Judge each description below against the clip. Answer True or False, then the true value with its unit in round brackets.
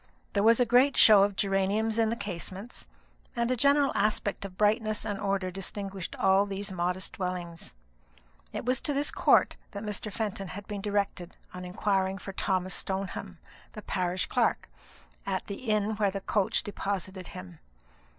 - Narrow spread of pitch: True (2.3 semitones)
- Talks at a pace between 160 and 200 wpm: True (165 wpm)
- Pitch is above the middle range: True (200 Hz)